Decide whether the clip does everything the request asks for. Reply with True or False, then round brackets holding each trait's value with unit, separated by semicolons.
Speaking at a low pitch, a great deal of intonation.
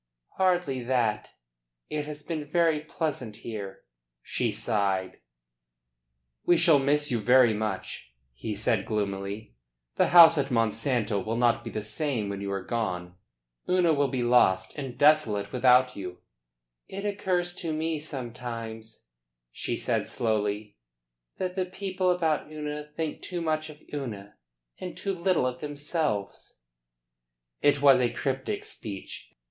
True (130 Hz; 6.4 semitones)